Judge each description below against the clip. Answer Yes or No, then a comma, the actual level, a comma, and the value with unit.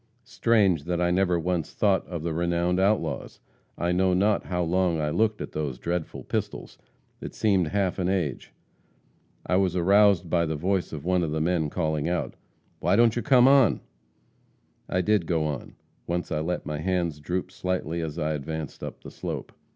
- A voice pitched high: No, very low, 90 Hz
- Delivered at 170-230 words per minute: Yes, average, 185 wpm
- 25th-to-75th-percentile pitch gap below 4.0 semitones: Yes, average, 3.0 semitones